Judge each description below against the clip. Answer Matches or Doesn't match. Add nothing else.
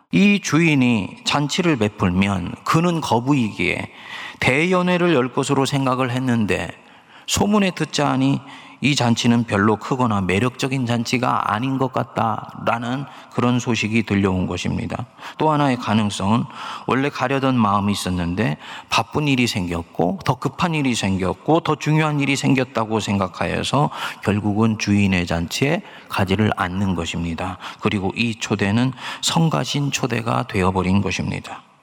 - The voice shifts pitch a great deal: Matches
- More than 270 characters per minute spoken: Matches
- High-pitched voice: Doesn't match